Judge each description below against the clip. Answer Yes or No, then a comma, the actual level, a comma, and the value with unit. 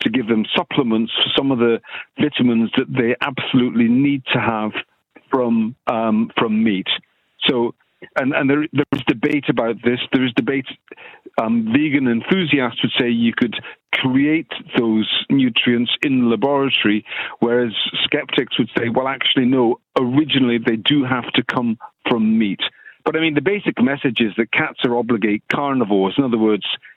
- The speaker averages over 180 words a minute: No, average, 165 wpm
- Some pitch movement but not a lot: Yes, average, 4.1 semitones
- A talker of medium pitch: No, low, 125 Hz